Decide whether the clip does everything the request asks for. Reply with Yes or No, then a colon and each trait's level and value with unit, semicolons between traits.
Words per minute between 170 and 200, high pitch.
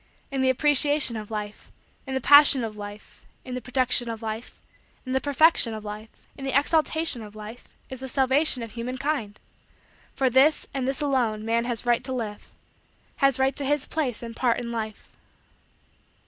Yes: average, 185 wpm; very high, 250 Hz